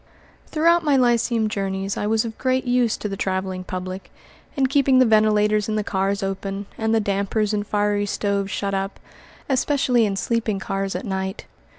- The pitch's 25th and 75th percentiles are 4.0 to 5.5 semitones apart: No, average, 3.2 semitones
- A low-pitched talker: No, high, 210 Hz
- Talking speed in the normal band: Yes, average, 180 wpm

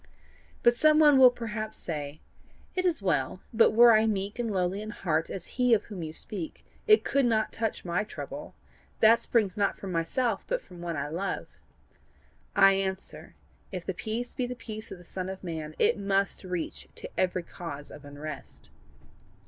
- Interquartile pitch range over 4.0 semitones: Yes, average, 4.6 semitones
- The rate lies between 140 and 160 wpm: No, average, 185 wpm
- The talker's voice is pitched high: Yes, high, 195 Hz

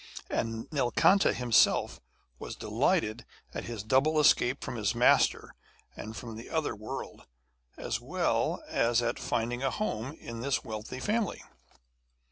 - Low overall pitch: Yes, low, 120 Hz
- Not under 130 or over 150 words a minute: Yes, slow, 135 wpm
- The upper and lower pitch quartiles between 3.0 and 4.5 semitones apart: Yes, average, 3.4 semitones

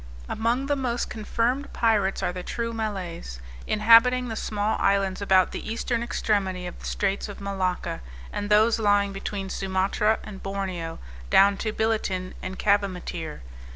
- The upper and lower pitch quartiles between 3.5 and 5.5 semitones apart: No, average, 2.8 semitones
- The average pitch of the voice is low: No, high, 205 Hz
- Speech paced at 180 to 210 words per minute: No, average, 150 wpm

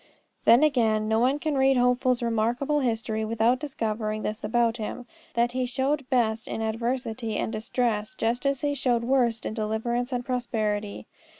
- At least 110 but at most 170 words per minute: Yes, average, 165 wpm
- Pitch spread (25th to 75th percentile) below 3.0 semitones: Yes, narrow, 2.5 semitones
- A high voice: Yes, high, 235 Hz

